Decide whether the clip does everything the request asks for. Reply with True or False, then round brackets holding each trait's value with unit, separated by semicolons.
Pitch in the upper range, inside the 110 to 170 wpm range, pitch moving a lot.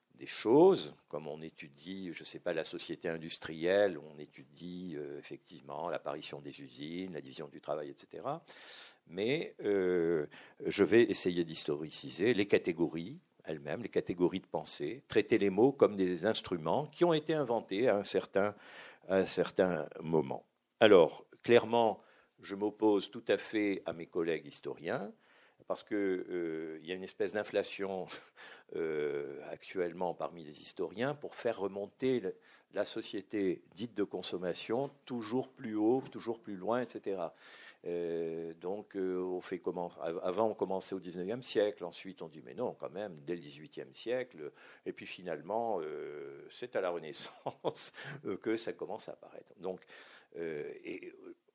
False (100 Hz; 155 wpm; 7.1 semitones)